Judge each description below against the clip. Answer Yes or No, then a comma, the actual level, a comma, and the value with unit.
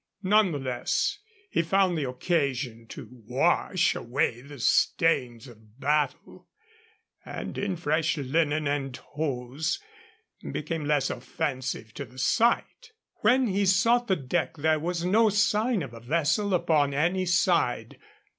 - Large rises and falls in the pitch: Yes, wide, 5.7 semitones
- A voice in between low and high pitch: Yes, medium, 155 Hz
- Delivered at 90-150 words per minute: Yes, slow, 135 wpm